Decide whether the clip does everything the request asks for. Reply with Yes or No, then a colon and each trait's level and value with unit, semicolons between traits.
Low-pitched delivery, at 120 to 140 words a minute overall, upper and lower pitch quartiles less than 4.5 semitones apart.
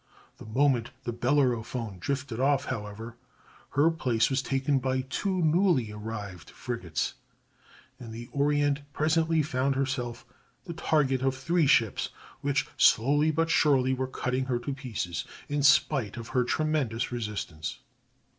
Yes: low, 130 Hz; slow, 135 wpm; average, 3.8 semitones